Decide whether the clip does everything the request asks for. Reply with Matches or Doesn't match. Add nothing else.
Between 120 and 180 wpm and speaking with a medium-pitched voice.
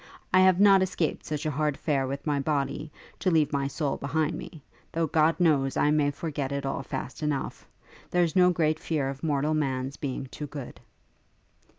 Doesn't match